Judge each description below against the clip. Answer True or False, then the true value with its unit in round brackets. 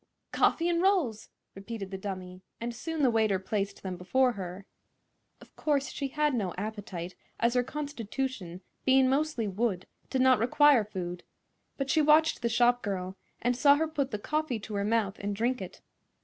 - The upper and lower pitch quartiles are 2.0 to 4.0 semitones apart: False (5.6 semitones)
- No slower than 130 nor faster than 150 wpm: False (175 wpm)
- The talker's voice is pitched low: False (235 Hz)